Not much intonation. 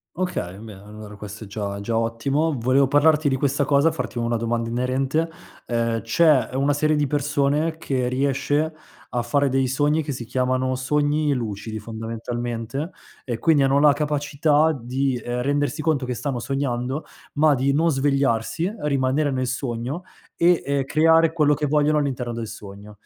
No: average, 3.8 semitones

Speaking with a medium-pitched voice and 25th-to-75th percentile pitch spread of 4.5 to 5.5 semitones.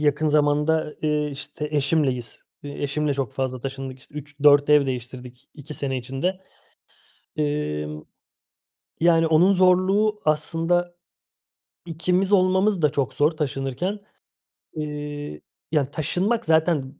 No: medium, 150 Hz; average, 3.3 semitones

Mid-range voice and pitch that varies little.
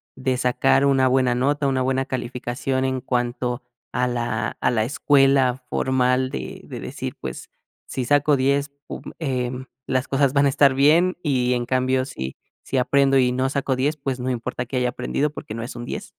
No: low, 130 Hz; narrow, 1.8 semitones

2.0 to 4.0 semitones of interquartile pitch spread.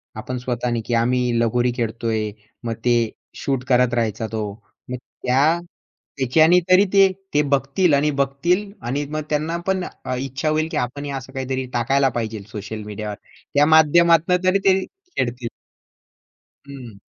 No: average, 4.4 semitones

